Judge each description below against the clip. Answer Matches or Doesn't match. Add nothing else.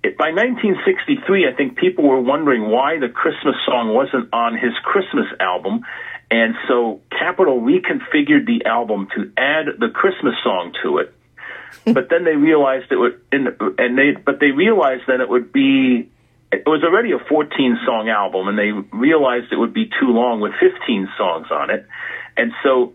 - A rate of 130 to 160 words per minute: Doesn't match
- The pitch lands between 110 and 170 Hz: Matches